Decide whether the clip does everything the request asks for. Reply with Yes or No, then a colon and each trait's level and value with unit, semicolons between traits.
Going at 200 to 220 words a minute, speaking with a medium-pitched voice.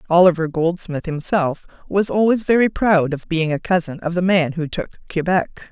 No: average, 180 wpm; medium, 175 Hz